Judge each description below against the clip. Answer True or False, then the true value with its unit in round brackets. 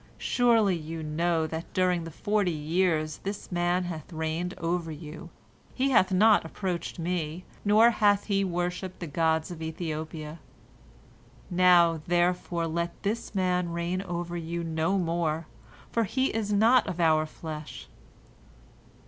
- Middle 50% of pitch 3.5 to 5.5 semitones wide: False (2.6 semitones)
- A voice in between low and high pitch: True (175 Hz)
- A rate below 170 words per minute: True (140 wpm)